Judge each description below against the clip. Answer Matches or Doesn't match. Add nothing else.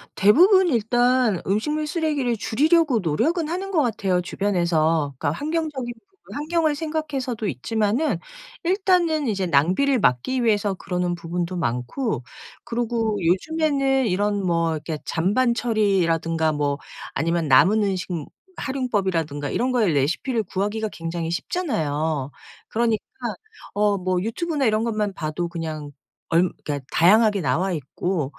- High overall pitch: Matches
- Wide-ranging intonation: Matches